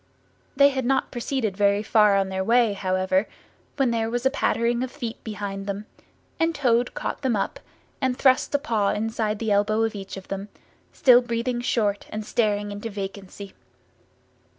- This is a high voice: Yes, high, 220 Hz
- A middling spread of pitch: Yes, average, 3.2 semitones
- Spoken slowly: No, average, 175 wpm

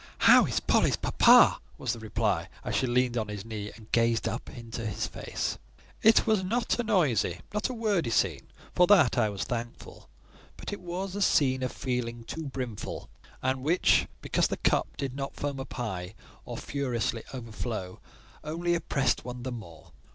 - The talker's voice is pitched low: Yes, low, 125 Hz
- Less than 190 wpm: Yes, average, 180 wpm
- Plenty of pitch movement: Yes, wide, 5.9 semitones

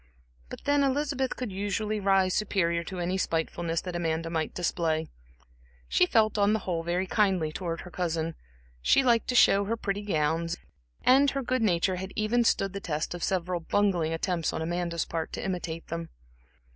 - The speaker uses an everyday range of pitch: Yes, average, 3.9 semitones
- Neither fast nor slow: Yes, average, 180 wpm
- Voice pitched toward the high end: No, medium, 180 Hz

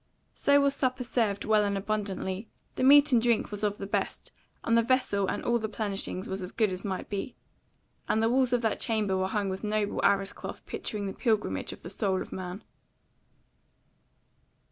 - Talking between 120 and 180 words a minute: No, average, 195 wpm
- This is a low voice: No, high, 210 Hz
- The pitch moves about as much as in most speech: Yes, average, 3.1 semitones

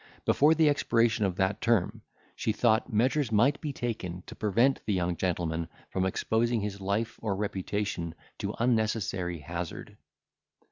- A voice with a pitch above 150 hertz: No, low, 105 Hz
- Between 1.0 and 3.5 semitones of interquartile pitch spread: No, average, 4.2 semitones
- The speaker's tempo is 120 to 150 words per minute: Yes, average, 145 wpm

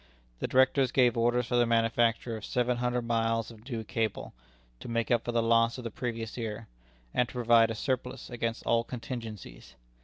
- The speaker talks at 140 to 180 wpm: No, average, 190 wpm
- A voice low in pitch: Yes, low, 115 Hz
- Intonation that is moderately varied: No, narrow, 1.3 semitones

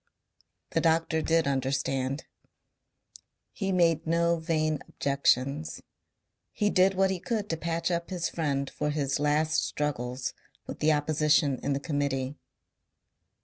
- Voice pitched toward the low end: No, medium, 155 Hz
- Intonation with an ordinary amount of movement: Yes, average, 3.2 semitones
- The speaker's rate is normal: No, slow, 130 wpm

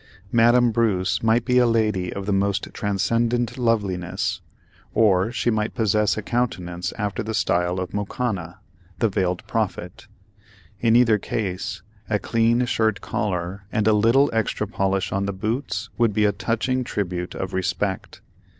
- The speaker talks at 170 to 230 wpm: No, average, 150 wpm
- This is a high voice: No, low, 105 Hz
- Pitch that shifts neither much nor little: Yes, average, 3.3 semitones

